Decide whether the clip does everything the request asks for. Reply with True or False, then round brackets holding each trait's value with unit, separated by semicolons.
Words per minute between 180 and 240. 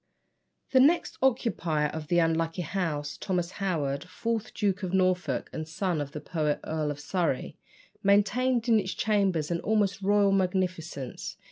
False (150 wpm)